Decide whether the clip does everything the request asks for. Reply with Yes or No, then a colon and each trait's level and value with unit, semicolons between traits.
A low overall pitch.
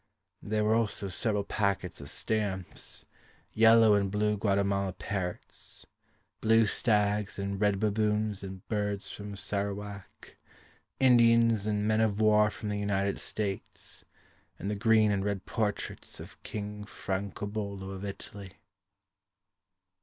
Yes: low, 105 Hz